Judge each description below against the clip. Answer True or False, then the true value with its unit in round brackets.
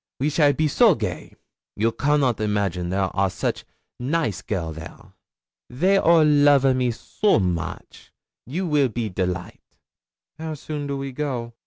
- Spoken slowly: False (155 wpm)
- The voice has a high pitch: False (130 Hz)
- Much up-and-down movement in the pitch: True (6.7 semitones)